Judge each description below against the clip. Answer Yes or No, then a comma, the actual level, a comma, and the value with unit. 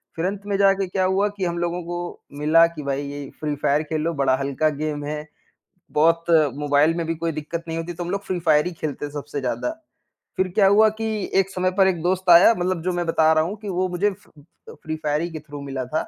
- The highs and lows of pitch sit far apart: No, average, 3.6 semitones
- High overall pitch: No, medium, 165 Hz